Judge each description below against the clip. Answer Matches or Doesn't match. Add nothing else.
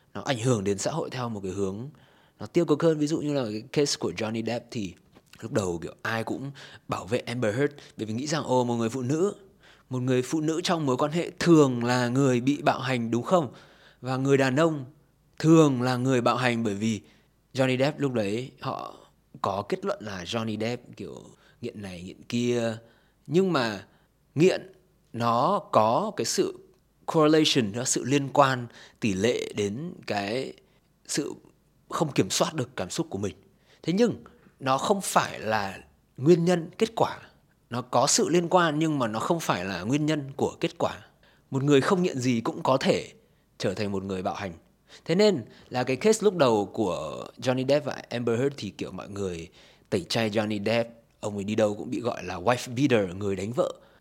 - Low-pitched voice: Matches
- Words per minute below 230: Matches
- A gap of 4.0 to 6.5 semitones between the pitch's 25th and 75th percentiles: Matches